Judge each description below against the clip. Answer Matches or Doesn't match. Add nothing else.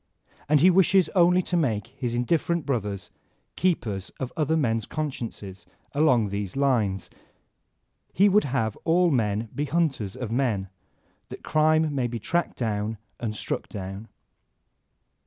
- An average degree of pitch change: Doesn't match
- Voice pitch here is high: Doesn't match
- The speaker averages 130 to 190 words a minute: Matches